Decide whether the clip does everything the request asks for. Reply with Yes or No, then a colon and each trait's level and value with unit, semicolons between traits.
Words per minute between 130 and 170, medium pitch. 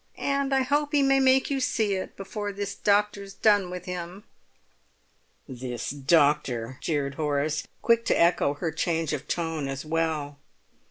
Yes: average, 155 wpm; medium, 170 Hz